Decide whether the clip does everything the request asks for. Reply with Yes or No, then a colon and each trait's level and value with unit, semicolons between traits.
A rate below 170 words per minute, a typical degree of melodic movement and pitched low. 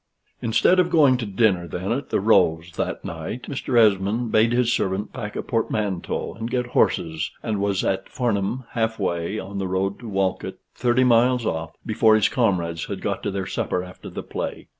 No: average, 190 wpm; average, 4.2 semitones; low, 105 Hz